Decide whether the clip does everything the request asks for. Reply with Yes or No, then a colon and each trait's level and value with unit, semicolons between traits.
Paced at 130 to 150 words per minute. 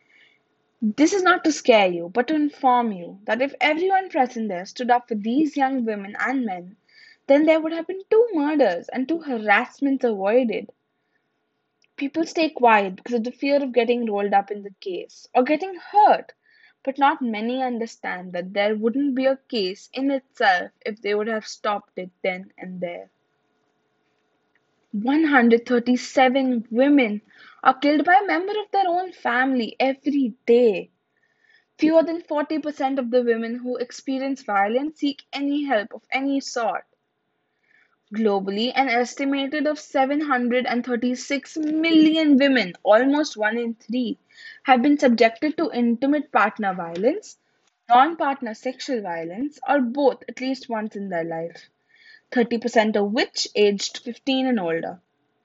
Yes: average, 145 wpm